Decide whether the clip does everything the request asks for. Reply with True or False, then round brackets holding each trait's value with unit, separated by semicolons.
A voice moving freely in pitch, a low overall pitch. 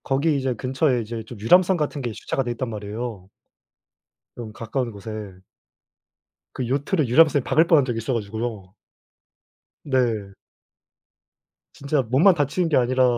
False (4.2 semitones; 125 Hz)